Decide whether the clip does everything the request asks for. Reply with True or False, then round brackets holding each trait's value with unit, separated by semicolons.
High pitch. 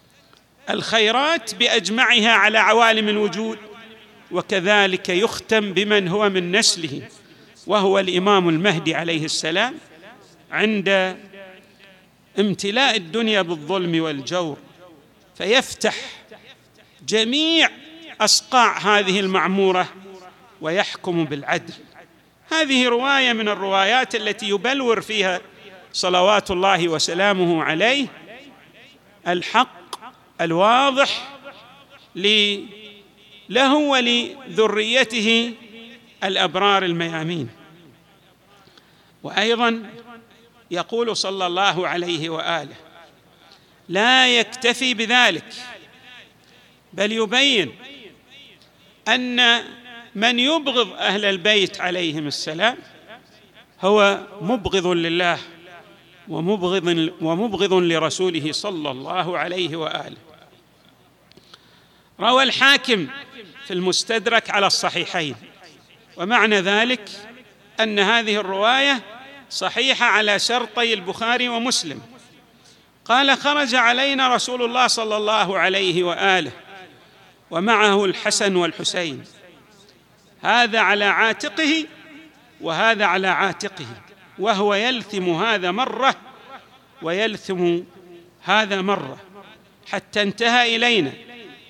True (205 Hz)